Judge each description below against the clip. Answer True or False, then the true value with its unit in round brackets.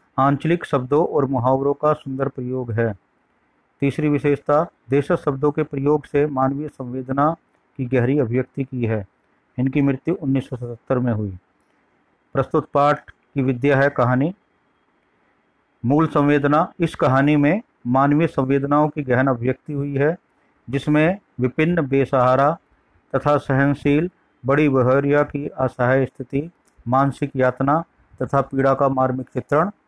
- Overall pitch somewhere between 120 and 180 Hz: True (140 Hz)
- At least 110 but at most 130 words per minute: True (125 wpm)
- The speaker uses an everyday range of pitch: False (2.1 semitones)